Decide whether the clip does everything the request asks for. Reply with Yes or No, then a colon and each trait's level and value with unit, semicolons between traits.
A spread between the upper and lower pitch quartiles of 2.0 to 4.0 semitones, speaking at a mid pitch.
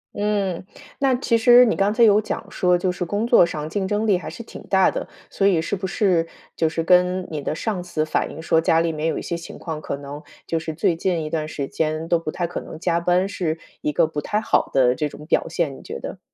Yes: average, 3.7 semitones; medium, 170 Hz